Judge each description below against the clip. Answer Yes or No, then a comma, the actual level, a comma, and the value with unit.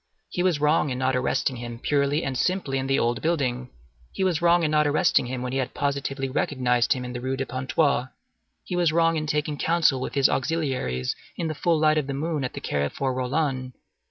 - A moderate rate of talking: No, fast, 215 wpm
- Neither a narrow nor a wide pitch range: Yes, average, 3.3 semitones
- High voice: No, medium, 140 Hz